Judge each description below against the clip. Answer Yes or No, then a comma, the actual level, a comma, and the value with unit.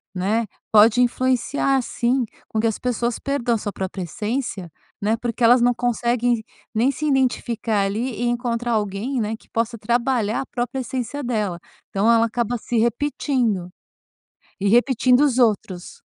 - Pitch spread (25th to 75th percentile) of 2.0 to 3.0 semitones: Yes, narrow, 2.4 semitones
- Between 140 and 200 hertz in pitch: No, high, 235 Hz